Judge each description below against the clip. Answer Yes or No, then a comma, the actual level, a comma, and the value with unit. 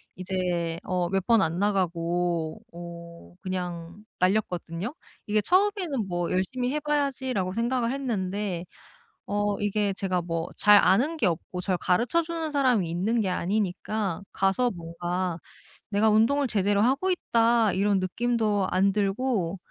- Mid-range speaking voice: No, high, 200 Hz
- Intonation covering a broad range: No, average, 4.7 semitones